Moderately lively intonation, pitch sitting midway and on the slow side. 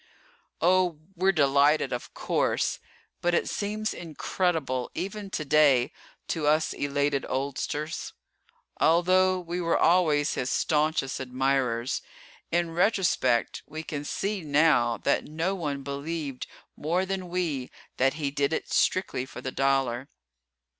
Yes: average, 4.2 semitones; medium, 155 Hz; slow, 125 wpm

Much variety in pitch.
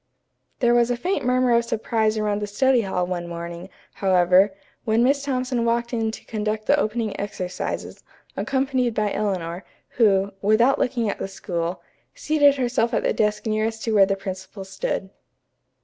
No: average, 3.7 semitones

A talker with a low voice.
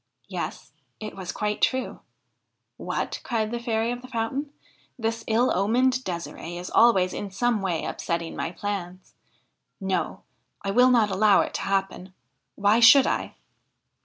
No: high, 215 Hz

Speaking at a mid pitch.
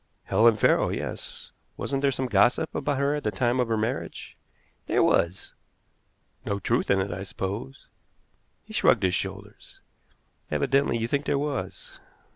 No: low, 115 Hz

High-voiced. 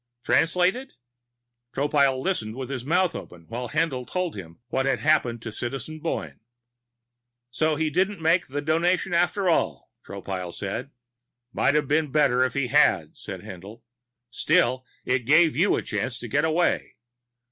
No: medium, 145 Hz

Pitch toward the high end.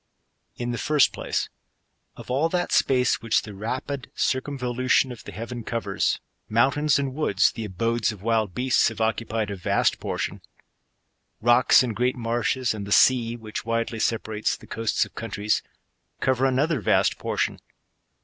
No: low, 120 Hz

